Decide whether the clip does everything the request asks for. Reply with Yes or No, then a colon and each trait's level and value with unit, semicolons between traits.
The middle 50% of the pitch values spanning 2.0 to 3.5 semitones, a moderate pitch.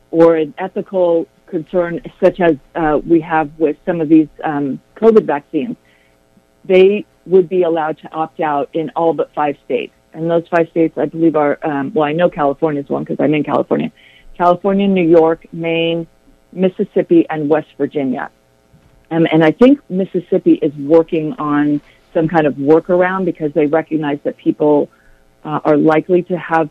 Yes: narrow, 2.6 semitones; medium, 160 Hz